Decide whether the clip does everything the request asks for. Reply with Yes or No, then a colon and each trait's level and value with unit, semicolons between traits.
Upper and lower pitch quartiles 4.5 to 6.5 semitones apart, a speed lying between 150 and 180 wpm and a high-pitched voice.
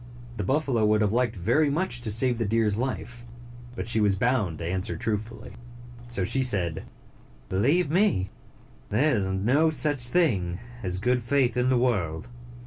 No: average, 4.8 semitones; average, 170 wpm; low, 115 Hz